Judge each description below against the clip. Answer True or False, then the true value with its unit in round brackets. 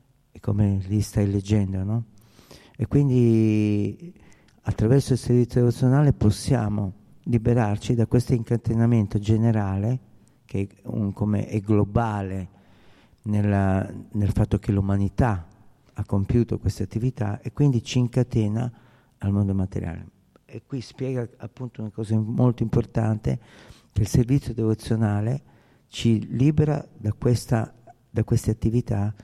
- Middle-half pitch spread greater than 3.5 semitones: False (3.0 semitones)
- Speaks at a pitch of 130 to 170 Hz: False (110 Hz)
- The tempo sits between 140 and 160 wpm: False (120 wpm)